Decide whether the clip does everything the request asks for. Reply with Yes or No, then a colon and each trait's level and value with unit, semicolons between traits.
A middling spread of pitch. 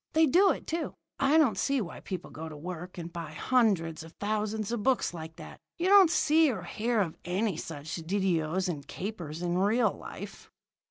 No: wide, 6.6 semitones